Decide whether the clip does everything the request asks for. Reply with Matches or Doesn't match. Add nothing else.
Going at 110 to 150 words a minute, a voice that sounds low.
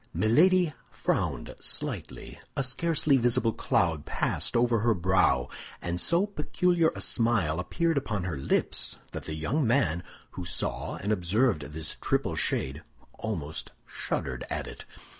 Matches